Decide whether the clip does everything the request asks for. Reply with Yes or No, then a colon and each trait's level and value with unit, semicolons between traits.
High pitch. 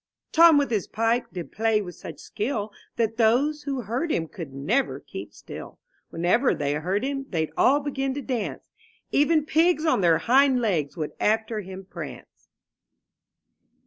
Yes: high, 225 Hz